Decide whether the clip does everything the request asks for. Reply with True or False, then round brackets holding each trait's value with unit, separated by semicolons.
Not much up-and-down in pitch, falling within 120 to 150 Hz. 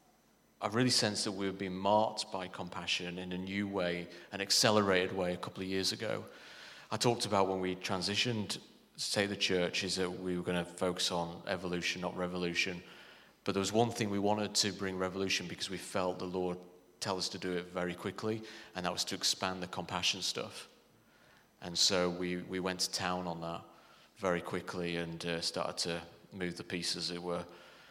False (2.0 semitones; 90 Hz)